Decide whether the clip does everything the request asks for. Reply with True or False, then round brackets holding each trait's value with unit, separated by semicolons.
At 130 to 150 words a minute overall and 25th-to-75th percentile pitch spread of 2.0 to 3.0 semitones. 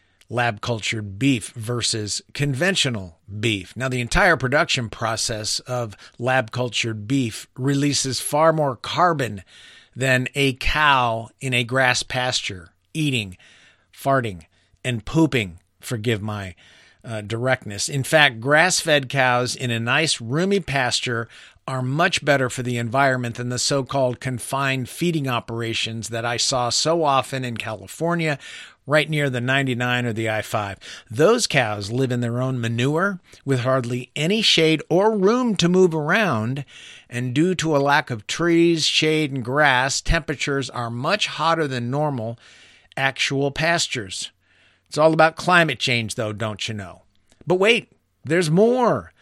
False (145 wpm; 4.7 semitones)